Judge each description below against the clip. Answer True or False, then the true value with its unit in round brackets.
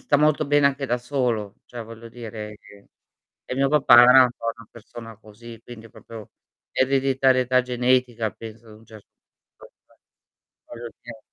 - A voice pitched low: True (120 Hz)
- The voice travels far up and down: False (2.4 semitones)